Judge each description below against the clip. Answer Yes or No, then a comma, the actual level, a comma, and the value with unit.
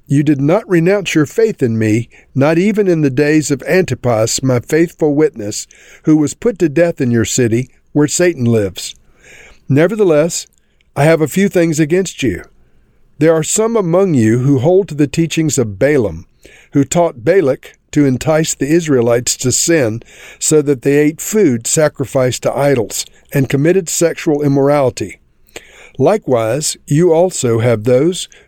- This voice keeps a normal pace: Yes, average, 160 wpm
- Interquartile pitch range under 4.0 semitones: No, average, 4.7 semitones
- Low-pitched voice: No, medium, 150 Hz